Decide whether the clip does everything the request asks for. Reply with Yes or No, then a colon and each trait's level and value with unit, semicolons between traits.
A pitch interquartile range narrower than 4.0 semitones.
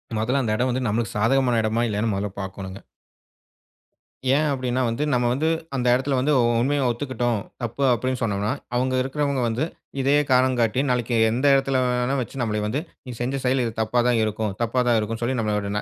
Yes: average, 2.8 semitones